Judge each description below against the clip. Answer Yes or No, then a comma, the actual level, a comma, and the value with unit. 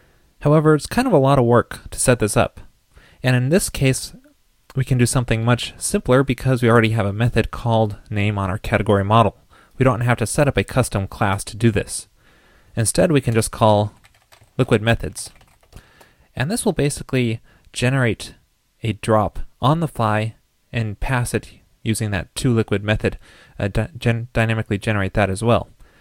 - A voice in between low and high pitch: No, low, 115 Hz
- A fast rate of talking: No, average, 180 wpm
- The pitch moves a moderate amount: Yes, average, 3.5 semitones